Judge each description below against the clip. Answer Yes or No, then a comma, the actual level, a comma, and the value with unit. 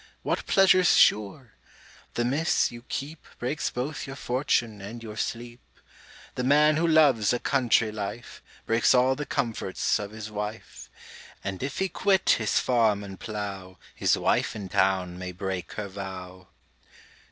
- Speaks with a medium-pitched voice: No, low, 115 Hz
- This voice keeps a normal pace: Yes, average, 150 wpm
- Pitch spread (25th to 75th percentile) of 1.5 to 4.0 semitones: No, average, 5.1 semitones